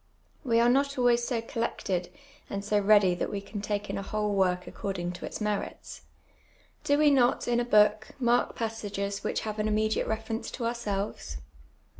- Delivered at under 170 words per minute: No, average, 180 wpm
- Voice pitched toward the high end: Yes, high, 215 Hz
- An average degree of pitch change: Yes, average, 3.0 semitones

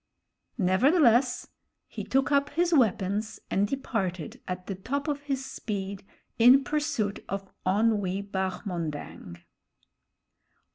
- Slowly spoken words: Yes, slow, 105 wpm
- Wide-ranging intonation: Yes, wide, 6.2 semitones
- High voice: Yes, high, 215 Hz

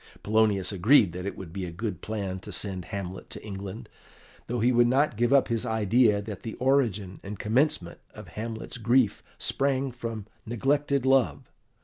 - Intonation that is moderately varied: Yes, average, 4.1 semitones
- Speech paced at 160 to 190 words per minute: Yes, average, 170 wpm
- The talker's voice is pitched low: Yes, low, 110 Hz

